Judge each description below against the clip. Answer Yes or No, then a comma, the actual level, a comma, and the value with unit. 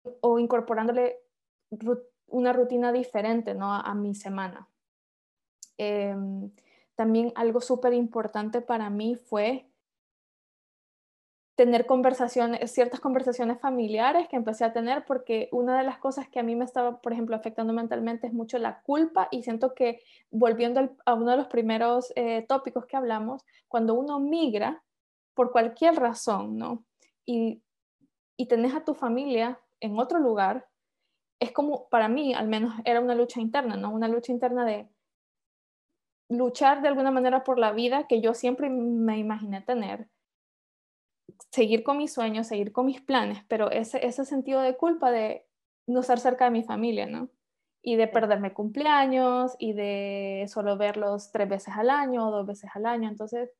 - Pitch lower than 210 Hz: No, high, 240 Hz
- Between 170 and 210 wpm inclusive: No, average, 160 wpm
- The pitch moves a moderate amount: No, narrow, 2.2 semitones